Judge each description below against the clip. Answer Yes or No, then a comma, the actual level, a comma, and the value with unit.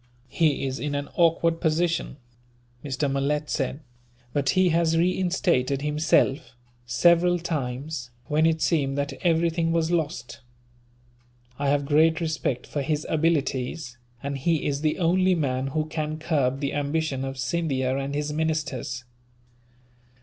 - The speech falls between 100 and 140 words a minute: Yes, slow, 135 wpm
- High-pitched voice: No, medium, 150 Hz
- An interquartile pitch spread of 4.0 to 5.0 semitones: No, average, 3.1 semitones